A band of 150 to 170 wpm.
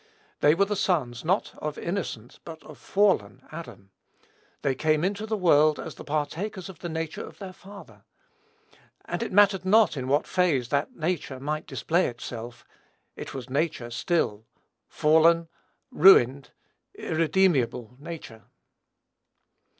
No: slow, 135 wpm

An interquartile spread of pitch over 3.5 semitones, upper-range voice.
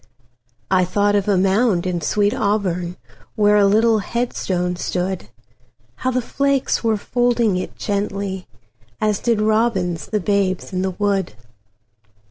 No: average, 3.2 semitones; high, 200 Hz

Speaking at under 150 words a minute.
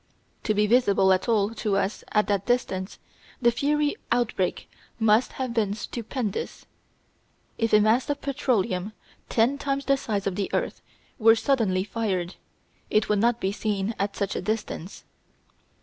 No: average, 155 wpm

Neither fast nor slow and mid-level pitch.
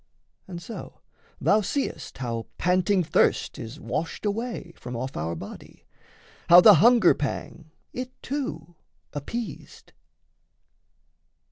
No: slow, 110 wpm; medium, 175 Hz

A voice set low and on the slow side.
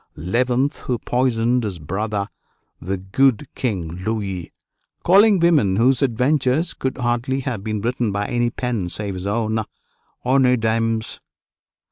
Yes: low, 115 Hz; slow, 125 wpm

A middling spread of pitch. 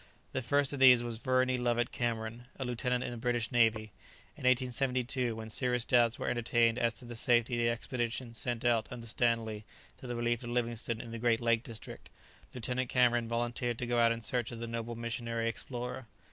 No: narrow, 1.1 semitones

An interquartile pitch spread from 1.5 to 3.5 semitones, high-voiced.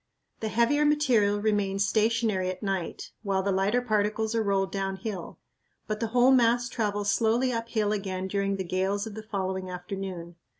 Yes: average, 2.9 semitones; high, 205 Hz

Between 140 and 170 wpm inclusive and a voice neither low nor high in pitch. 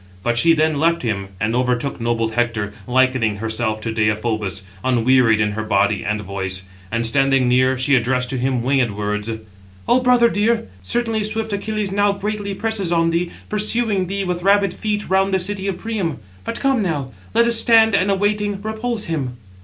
No: average, 180 wpm; medium, 145 Hz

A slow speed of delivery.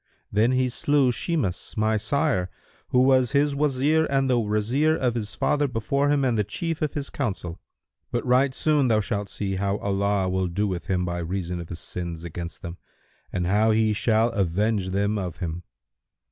No: average, 190 wpm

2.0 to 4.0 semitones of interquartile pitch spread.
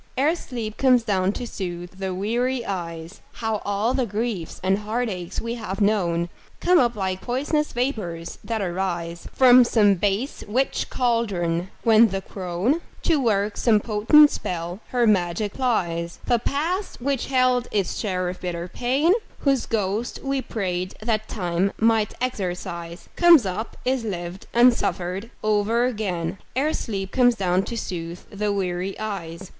No: average, 5.0 semitones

